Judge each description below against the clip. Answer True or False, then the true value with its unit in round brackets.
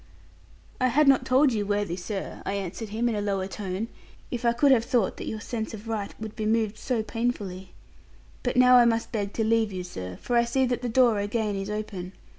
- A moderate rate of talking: False (230 wpm)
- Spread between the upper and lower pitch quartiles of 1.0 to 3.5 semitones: True (3.1 semitones)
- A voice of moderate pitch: False (220 Hz)